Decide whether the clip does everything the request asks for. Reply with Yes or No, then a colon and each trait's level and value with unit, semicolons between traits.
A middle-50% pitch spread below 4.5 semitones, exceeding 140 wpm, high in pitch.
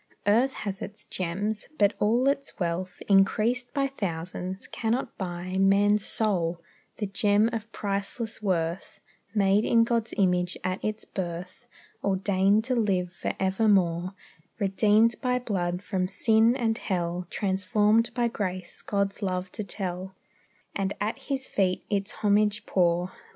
No: average, 3.1 semitones; slow, 135 wpm; high, 200 Hz